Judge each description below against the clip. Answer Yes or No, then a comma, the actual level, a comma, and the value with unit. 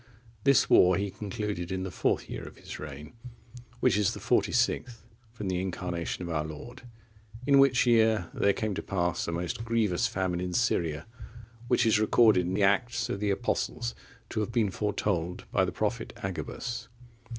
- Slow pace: No, average, 180 wpm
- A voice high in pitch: No, very low, 95 Hz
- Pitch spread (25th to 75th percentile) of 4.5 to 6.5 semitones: No, average, 4.1 semitones